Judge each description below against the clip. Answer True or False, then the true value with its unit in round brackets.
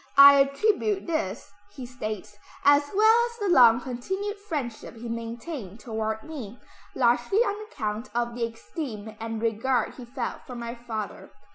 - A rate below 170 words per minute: True (150 wpm)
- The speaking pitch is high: True (245 Hz)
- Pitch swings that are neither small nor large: False (5.8 semitones)